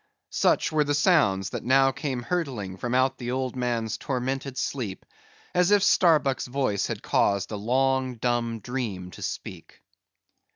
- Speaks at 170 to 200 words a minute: No, average, 155 wpm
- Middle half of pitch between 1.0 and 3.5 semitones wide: Yes, average, 3.1 semitones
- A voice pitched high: No, low, 130 Hz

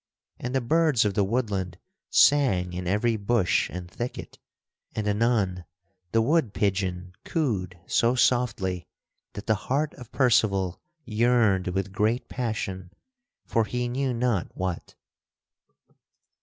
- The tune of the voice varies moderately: Yes, average, 4.7 semitones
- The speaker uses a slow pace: Yes, slow, 125 wpm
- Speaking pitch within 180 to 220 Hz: No, low, 110 Hz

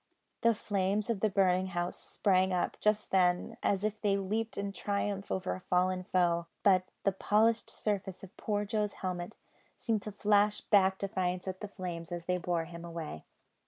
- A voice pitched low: No, high, 190 Hz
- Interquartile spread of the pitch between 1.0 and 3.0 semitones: Yes, narrow, 2.4 semitones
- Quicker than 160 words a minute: Yes, average, 180 wpm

